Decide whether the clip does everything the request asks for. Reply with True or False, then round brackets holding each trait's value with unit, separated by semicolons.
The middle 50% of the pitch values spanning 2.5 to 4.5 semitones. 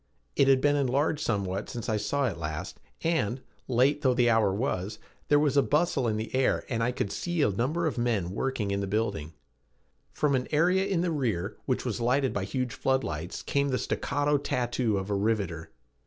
False (5.5 semitones)